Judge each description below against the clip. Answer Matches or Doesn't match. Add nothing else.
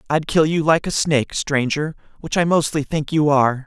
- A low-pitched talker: Doesn't match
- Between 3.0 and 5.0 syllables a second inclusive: Doesn't match